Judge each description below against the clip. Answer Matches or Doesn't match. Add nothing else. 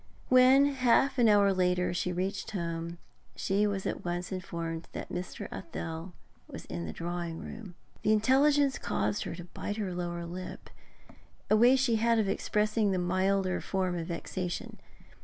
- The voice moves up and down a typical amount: Matches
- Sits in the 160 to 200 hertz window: Matches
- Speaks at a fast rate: Doesn't match